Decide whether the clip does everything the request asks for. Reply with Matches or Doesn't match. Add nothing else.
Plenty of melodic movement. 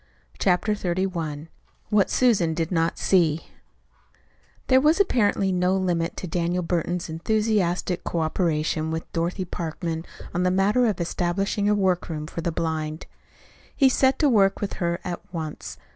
Doesn't match